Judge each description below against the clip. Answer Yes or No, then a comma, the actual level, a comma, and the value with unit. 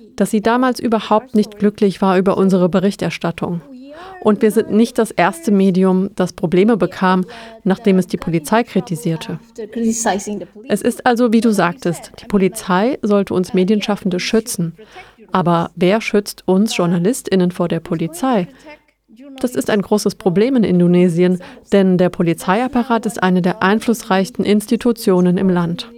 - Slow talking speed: No, average, 145 wpm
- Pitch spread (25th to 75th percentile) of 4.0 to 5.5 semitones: No, average, 3.6 semitones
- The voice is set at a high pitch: Yes, high, 200 Hz